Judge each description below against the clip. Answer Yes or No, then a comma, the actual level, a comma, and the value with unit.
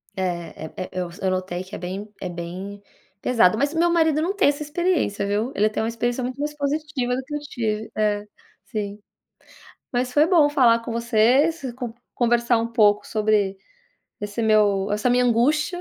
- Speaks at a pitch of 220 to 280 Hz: Yes, high, 230 Hz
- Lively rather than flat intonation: Yes, wide, 5.7 semitones